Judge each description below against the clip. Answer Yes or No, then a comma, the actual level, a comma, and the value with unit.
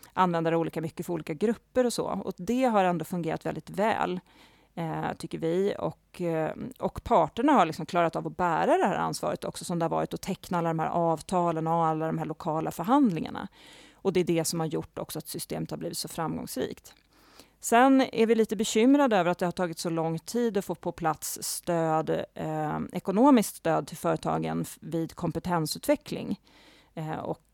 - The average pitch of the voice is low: No, medium, 175 Hz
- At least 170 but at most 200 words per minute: Yes, fast, 195 wpm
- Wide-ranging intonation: No, average, 4.3 semitones